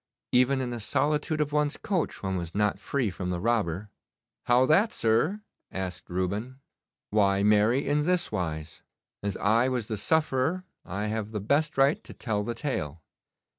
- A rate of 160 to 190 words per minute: Yes, average, 170 wpm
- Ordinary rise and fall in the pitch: No, wide, 6.2 semitones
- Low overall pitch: Yes, low, 115 Hz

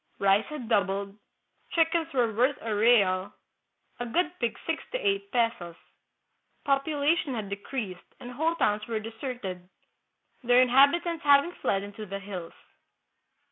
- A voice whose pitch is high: Yes, high, 235 Hz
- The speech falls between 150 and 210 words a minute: No, average, 140 wpm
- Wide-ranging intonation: Yes, wide, 6.1 semitones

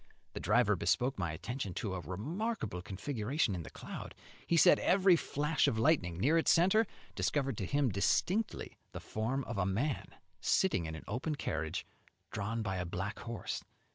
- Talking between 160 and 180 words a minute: Yes, average, 170 wpm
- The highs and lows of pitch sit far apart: Yes, wide, 8.2 semitones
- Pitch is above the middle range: No, low, 115 Hz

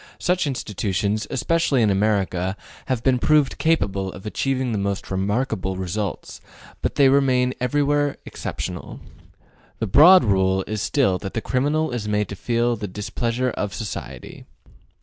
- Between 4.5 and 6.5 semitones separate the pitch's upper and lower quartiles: Yes, average, 5.2 semitones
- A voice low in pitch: Yes, low, 115 Hz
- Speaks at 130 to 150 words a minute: Yes, average, 145 wpm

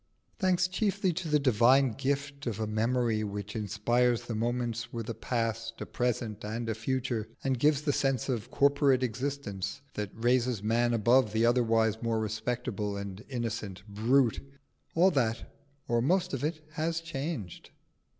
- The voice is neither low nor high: No, low, 120 Hz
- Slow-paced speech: No, average, 155 wpm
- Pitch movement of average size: Yes, average, 3.8 semitones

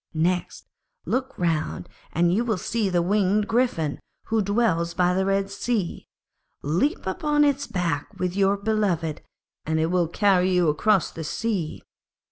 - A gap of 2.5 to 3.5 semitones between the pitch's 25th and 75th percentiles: No, average, 4.2 semitones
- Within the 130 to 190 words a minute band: Yes, average, 150 wpm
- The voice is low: No, high, 190 Hz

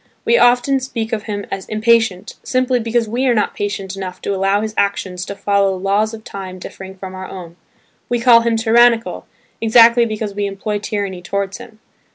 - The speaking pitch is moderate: No, high, 210 Hz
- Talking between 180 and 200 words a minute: Yes, average, 190 wpm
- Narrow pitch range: No, average, 3.0 semitones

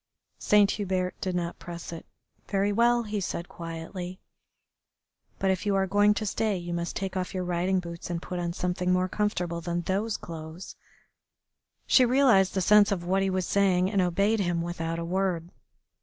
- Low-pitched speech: No, medium, 185 Hz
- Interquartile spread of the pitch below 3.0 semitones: Yes, narrow, 2.5 semitones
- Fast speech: No, average, 185 wpm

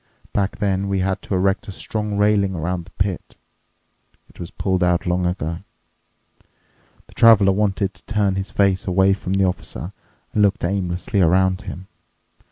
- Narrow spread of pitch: Yes, narrow, 1.6 semitones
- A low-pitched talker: Yes, very low, 95 Hz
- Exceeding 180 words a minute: No, average, 165 wpm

